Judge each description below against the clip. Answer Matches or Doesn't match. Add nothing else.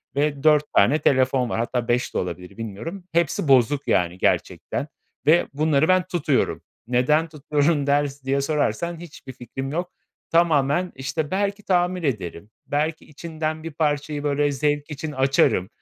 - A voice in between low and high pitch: Matches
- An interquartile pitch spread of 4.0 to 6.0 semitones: Doesn't match